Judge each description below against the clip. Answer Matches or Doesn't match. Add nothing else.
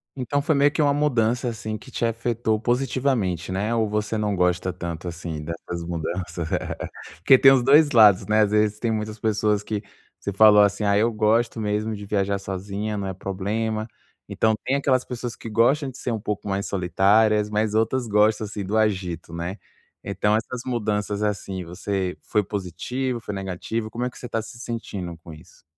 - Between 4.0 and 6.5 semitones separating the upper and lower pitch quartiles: Doesn't match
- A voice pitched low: Matches